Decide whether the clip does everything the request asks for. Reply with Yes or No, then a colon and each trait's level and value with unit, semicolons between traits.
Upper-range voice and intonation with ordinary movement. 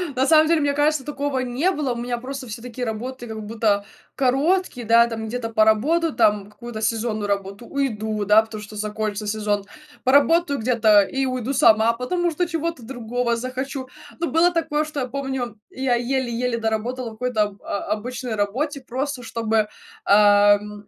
Yes: high, 240 Hz; average, 3.9 semitones